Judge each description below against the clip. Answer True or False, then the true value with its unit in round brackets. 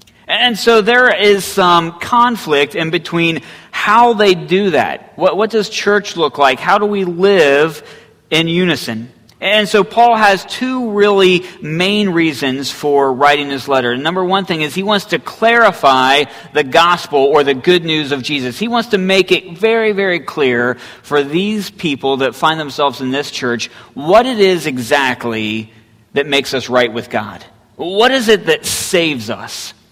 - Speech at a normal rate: True (170 wpm)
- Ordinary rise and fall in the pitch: False (6.9 semitones)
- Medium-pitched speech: True (165 Hz)